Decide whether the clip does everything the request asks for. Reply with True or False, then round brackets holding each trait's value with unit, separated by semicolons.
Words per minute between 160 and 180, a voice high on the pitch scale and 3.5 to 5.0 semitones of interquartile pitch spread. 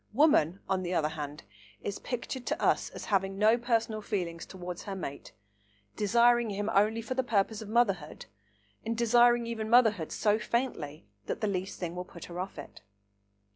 True (175 wpm; 210 Hz; 4.5 semitones)